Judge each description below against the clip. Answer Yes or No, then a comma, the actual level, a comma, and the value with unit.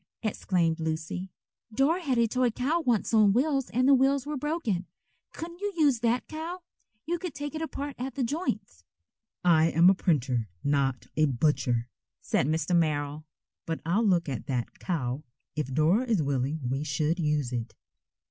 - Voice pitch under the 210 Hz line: Yes, medium, 185 Hz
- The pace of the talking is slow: No, average, 170 wpm